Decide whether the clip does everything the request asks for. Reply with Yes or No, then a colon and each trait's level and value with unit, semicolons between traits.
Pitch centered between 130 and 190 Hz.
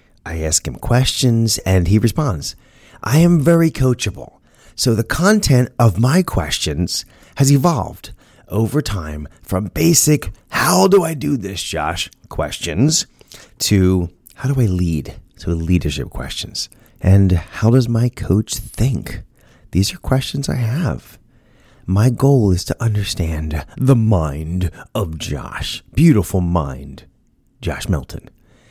No: low, 110 Hz